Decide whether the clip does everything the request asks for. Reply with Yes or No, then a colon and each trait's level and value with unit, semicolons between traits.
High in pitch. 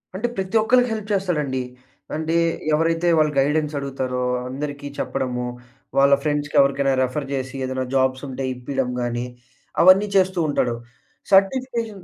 No: medium, 145 Hz